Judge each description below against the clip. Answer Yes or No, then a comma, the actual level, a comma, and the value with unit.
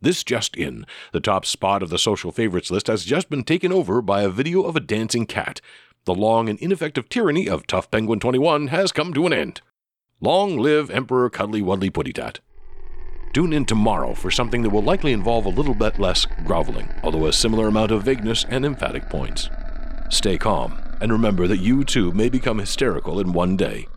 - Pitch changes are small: No, average, 4.6 semitones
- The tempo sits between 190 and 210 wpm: Yes, average, 200 wpm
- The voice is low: Yes, low, 115 Hz